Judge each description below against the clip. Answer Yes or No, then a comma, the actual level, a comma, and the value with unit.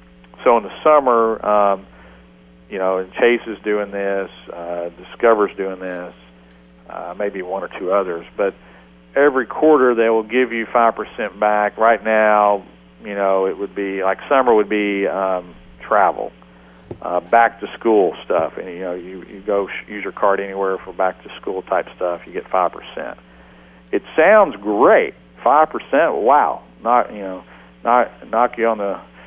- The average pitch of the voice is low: Yes, very low, 95 Hz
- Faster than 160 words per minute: Yes, average, 170 wpm